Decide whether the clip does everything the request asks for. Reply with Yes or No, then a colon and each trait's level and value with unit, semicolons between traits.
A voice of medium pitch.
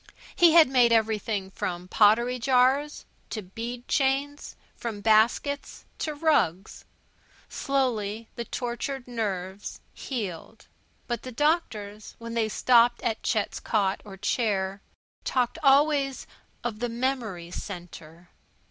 No: high, 230 Hz